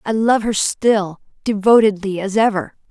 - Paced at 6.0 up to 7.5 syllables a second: No, 4.5 syllables/s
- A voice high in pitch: Yes, high, 210 Hz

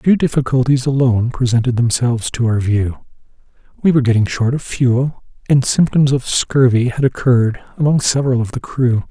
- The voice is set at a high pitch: No, low, 125 Hz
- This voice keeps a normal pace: Yes, average, 165 wpm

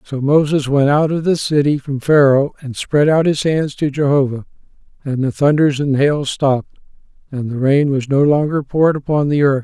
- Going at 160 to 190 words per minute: No, average, 200 wpm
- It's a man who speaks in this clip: Yes, male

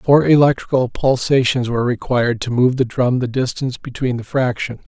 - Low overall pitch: Yes, low, 125 Hz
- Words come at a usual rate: Yes, average, 170 wpm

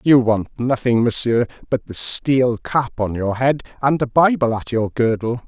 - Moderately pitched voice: No, low, 120 Hz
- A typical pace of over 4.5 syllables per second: No, 4.3 syllables/s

